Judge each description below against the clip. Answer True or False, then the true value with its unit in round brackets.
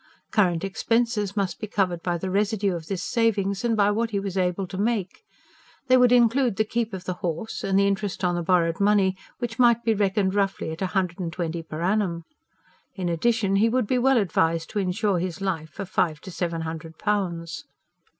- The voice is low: False (195 Hz)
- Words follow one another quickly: True (210 wpm)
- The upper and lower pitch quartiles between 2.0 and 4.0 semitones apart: True (3.6 semitones)